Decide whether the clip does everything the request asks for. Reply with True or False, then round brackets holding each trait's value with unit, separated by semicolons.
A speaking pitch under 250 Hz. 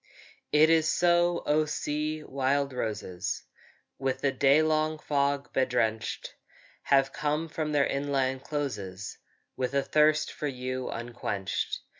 True (140 Hz)